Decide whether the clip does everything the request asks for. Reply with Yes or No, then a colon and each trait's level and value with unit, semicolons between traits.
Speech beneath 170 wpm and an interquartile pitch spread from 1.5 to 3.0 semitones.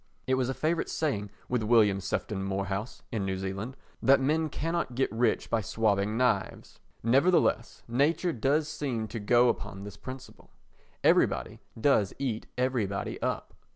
No: average, 150 wpm; average, 4.8 semitones